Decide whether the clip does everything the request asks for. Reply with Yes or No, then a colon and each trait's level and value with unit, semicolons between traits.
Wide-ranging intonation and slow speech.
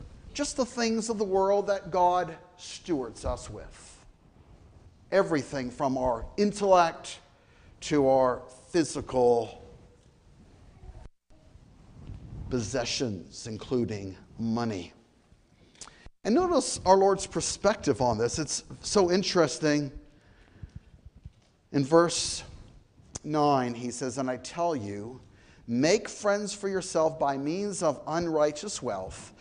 Yes: wide, 7.3 semitones; slow, 100 wpm